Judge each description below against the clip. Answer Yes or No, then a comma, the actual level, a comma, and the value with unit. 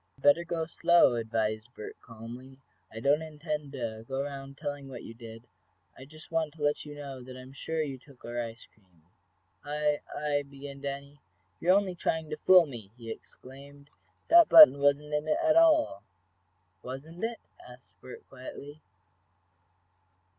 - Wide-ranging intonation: No, average, 3.4 semitones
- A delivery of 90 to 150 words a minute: No, average, 165 wpm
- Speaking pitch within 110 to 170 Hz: Yes, medium, 140 Hz